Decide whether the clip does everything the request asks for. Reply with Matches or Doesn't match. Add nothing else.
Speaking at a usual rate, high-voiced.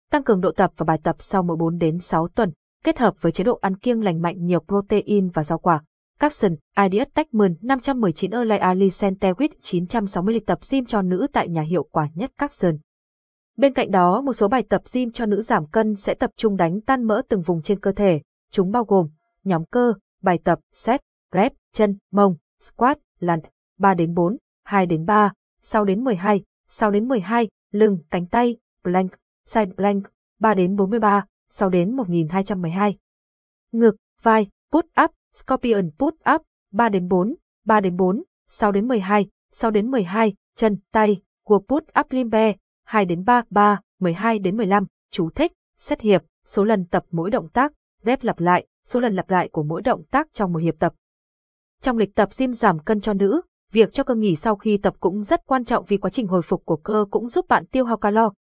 Matches